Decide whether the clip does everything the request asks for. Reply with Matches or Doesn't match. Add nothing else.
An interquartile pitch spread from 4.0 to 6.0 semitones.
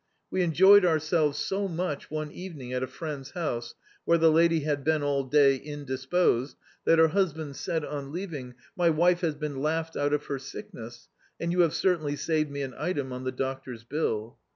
Doesn't match